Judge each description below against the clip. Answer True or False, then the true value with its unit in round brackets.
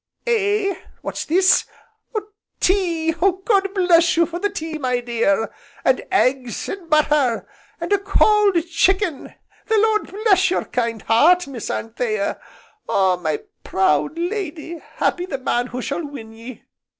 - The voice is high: True (330 Hz)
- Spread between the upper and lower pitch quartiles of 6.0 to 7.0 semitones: False (7.6 semitones)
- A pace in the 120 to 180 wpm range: True (140 wpm)